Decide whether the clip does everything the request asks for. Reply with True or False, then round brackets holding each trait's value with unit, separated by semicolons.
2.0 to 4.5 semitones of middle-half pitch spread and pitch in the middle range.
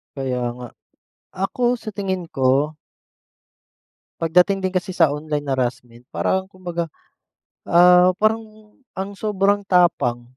False (5.4 semitones; 180 Hz)